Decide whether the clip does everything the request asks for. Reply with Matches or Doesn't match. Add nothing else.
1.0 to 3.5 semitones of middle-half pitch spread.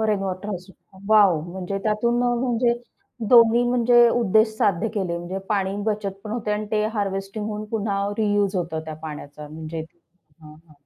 Matches